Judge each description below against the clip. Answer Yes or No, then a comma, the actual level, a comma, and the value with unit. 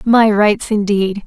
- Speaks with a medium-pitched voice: No, high, 210 Hz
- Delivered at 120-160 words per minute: Yes, average, 140 wpm